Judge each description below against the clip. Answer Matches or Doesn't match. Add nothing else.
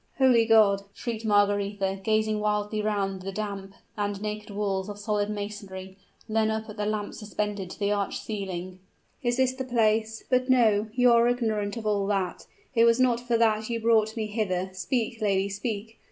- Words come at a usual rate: Matches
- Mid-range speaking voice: Doesn't match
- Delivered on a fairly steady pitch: Matches